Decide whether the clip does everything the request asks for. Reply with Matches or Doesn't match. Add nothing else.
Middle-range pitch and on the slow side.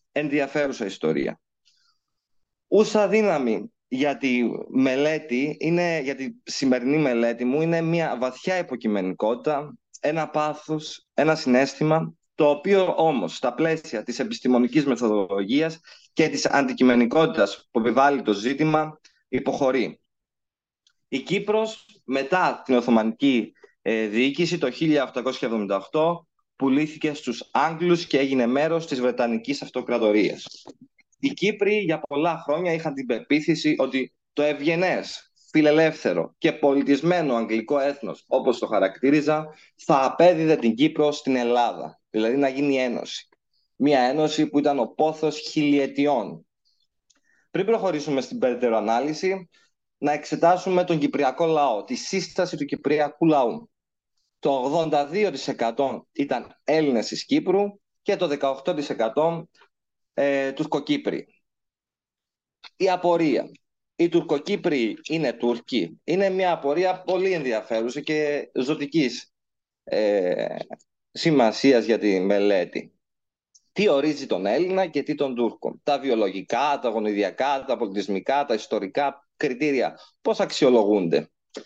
Matches